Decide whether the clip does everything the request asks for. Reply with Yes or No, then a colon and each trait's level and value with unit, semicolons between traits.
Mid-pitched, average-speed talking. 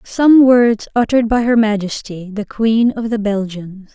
No: high, 220 Hz; average, 165 wpm